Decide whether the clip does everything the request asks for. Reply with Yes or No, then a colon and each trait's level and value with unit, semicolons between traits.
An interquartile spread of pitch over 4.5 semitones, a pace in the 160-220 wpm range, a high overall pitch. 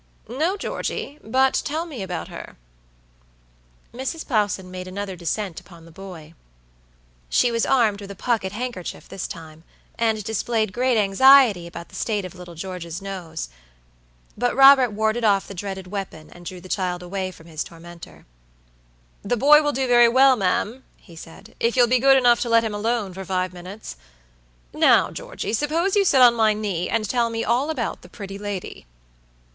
Yes: average, 5.0 semitones; average, 175 wpm; high, 210 Hz